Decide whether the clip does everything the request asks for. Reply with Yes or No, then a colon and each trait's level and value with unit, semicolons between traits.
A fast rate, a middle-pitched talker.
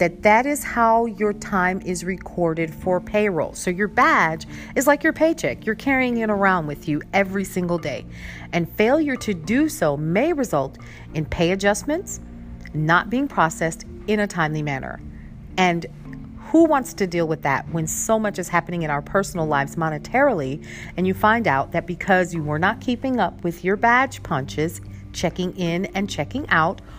No: average, 180 wpm; medium, 180 Hz